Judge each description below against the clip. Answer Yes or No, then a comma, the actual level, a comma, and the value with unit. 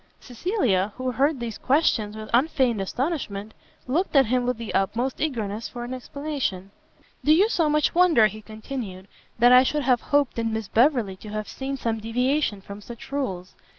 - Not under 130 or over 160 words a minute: No, average, 180 wpm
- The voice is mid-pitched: No, high, 245 Hz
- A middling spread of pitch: Yes, average, 4.4 semitones